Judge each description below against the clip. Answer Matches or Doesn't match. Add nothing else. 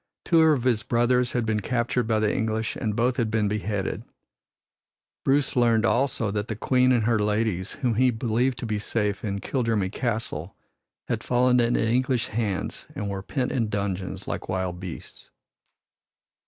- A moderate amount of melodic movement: Matches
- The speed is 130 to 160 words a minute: Doesn't match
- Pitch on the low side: Matches